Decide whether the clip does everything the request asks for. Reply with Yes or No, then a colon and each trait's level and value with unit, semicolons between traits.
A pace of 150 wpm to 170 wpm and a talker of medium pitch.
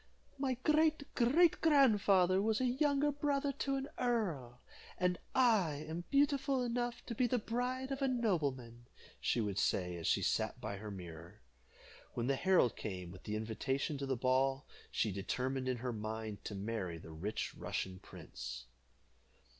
Yes: average, 160 wpm; medium, 150 Hz